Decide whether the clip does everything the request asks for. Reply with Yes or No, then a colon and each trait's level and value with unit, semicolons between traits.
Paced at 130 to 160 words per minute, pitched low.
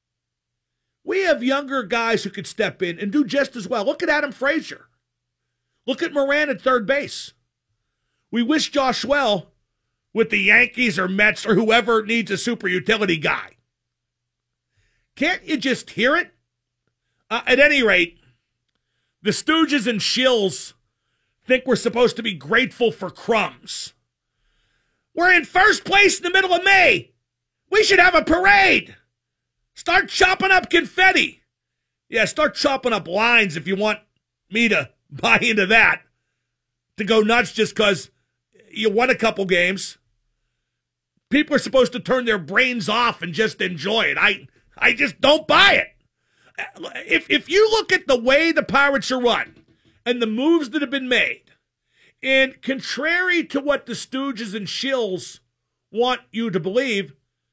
No: average, 155 wpm; high, 230 Hz